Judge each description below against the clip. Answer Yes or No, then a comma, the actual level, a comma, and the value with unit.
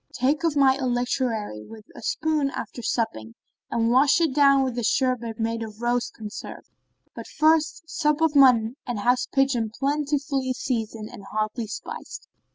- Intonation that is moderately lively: Yes, average, 3.8 semitones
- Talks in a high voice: Yes, very high, 250 Hz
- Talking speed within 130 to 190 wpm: Yes, average, 160 wpm